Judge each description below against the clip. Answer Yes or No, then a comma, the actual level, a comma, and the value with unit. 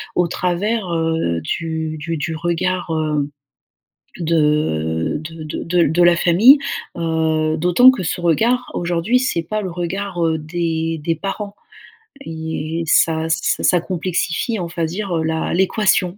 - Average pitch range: No, narrow, 2.3 semitones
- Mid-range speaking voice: Yes, medium, 165 Hz